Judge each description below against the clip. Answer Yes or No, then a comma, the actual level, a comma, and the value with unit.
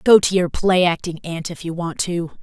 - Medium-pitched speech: Yes, medium, 175 Hz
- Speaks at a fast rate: Yes, fast, 250 wpm